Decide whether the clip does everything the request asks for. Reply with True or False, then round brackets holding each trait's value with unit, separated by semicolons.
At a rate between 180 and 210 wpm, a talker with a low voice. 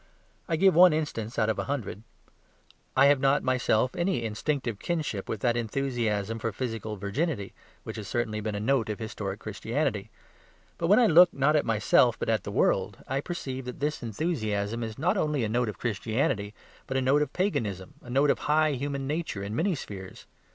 True (195 wpm; 125 Hz)